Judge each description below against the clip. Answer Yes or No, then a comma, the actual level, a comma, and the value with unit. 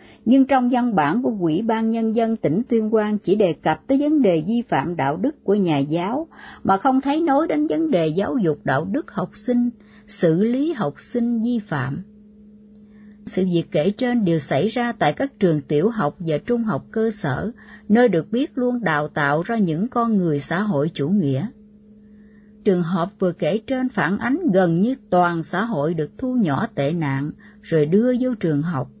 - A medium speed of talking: Yes, average, 200 wpm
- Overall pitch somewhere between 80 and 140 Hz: No, high, 210 Hz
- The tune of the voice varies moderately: No, wide, 5.9 semitones